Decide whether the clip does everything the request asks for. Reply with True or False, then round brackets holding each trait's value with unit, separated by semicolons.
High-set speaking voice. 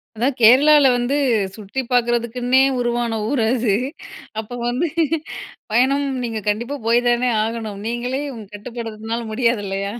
True (240 Hz)